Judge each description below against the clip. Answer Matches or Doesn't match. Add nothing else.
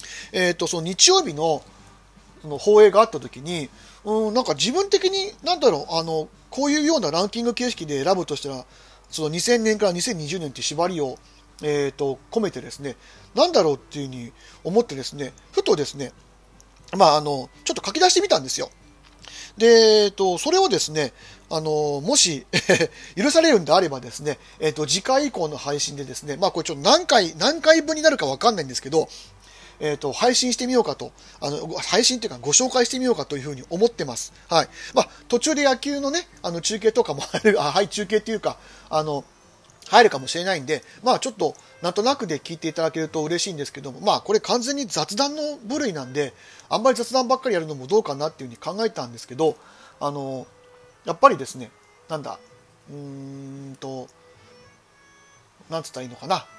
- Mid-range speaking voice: Matches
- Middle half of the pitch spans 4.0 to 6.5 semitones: Doesn't match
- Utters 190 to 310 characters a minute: Doesn't match